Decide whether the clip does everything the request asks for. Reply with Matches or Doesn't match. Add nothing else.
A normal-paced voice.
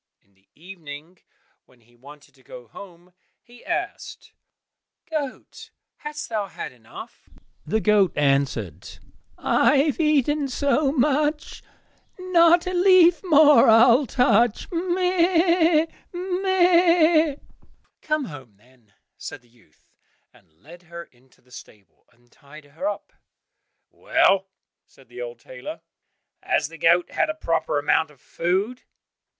Doesn't match